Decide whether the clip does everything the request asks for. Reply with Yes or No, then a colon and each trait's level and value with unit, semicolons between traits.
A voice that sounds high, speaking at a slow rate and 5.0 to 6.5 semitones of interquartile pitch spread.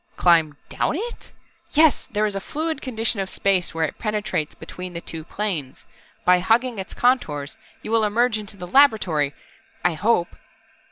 No: high, 205 Hz; average, 170 wpm; wide, 5.6 semitones